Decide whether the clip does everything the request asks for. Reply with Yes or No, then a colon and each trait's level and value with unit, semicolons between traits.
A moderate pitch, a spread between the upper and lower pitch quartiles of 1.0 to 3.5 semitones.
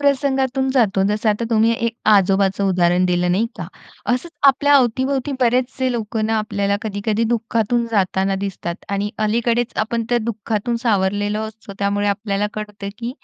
No: high, 215 Hz; average, 3.0 semitones